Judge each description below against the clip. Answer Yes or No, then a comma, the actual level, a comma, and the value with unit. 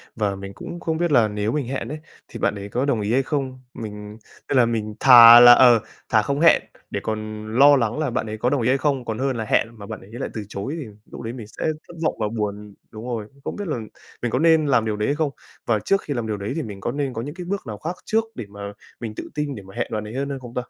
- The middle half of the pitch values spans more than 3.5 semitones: Yes, average, 4.6 semitones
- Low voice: Yes, low, 120 Hz